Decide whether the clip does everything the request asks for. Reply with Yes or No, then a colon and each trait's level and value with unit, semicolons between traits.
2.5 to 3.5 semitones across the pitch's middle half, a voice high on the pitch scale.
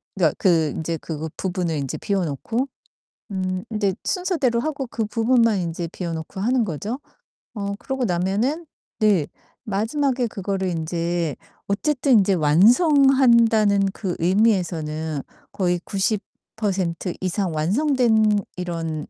No: average, 5.3 semitones; high, 195 Hz